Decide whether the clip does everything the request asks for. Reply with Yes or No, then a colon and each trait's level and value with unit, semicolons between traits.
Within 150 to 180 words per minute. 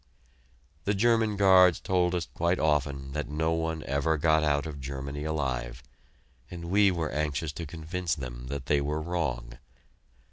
Yes: average, 155 wpm